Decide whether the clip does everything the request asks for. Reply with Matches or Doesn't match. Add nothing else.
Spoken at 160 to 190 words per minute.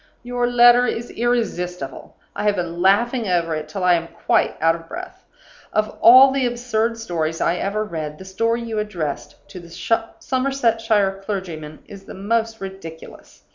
Matches